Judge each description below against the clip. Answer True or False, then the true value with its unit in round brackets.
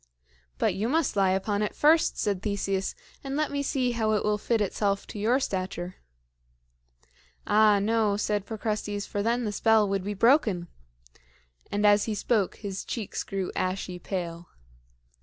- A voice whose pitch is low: False (205 Hz)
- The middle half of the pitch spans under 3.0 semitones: True (2.4 semitones)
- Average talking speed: True (160 wpm)